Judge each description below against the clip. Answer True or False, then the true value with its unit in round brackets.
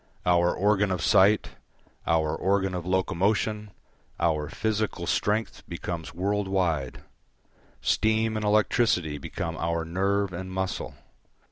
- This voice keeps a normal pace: False (115 wpm)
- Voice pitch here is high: False (95 Hz)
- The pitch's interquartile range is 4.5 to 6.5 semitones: False (3.4 semitones)